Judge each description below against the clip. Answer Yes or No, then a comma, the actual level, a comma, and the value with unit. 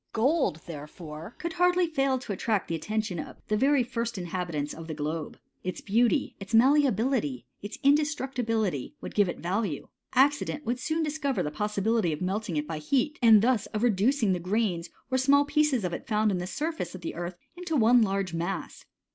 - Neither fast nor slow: Yes, average, 195 wpm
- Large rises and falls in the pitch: Yes, wide, 7.2 semitones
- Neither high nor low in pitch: No, high, 215 Hz